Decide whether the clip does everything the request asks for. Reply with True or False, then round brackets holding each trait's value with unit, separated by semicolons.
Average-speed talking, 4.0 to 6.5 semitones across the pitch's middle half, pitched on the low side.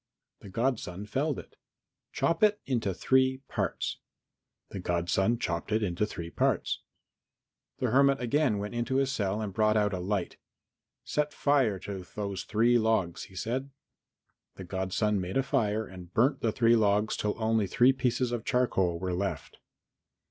True (160 wpm; 4.8 semitones; 110 Hz)